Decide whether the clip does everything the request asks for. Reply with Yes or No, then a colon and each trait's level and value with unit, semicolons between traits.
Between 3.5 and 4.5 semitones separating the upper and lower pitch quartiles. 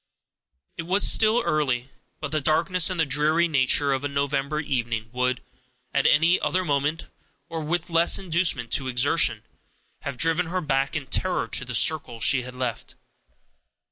Yes: average, 4.1 semitones